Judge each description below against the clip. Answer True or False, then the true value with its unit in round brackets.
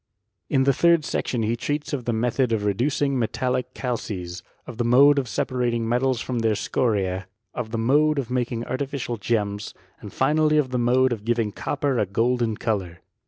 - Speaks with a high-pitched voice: False (120 Hz)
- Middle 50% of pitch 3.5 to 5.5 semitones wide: False (2.9 semitones)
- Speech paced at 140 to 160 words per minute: False (190 wpm)